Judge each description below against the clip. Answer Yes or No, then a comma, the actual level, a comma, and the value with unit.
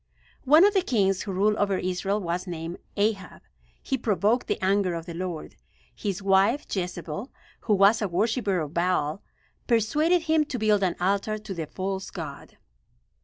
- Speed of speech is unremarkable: Yes, average, 170 wpm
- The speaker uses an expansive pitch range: No, average, 3.2 semitones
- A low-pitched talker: No, high, 195 Hz